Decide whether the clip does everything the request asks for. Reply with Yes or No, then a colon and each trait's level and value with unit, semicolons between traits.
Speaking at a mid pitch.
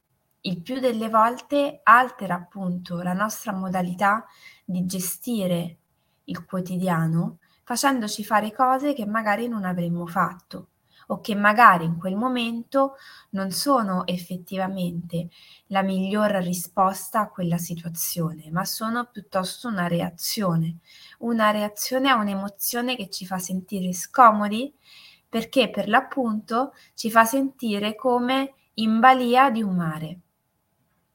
No: high, 205 Hz